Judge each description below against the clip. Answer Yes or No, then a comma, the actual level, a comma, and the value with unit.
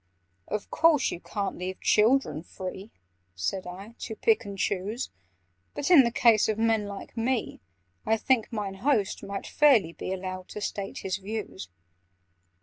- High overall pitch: Yes, high, 210 Hz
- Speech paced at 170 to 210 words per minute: No, average, 155 wpm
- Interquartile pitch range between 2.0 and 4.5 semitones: Yes, average, 3.4 semitones